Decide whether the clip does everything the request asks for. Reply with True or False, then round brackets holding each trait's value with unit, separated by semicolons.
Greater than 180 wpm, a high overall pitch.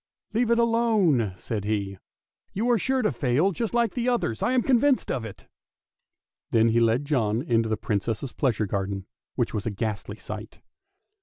False (200 wpm; 120 Hz)